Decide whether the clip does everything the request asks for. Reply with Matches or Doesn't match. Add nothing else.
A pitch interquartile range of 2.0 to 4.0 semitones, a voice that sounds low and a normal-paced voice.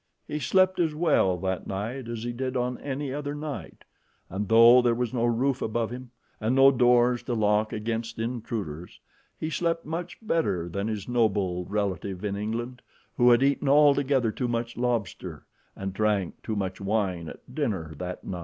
Doesn't match